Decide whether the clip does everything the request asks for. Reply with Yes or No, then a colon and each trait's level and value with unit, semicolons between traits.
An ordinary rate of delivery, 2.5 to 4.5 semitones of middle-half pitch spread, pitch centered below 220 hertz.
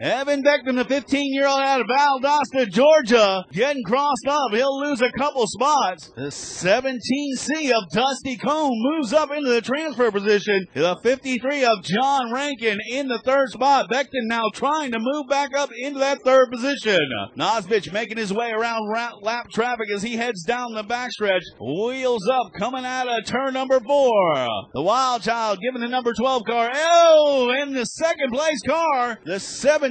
No: average, 170 wpm; average, 3.3 semitones; very high, 255 Hz